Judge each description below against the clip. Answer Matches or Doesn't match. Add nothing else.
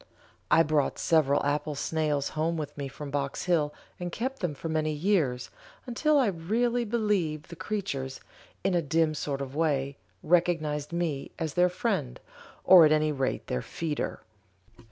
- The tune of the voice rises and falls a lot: Doesn't match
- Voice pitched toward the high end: Doesn't match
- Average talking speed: Matches